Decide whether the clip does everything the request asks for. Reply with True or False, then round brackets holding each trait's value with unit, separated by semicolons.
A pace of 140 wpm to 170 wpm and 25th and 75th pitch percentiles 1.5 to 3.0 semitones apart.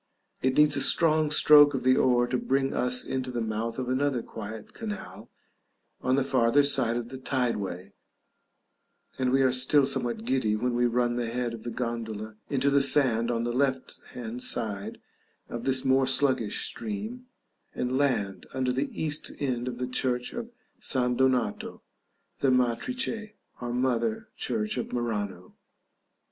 True (165 wpm; 2.4 semitones)